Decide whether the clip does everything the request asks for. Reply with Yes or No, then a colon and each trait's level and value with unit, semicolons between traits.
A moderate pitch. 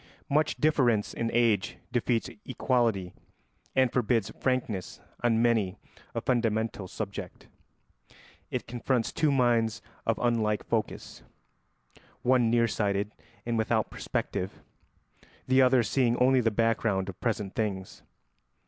No: low, 115 Hz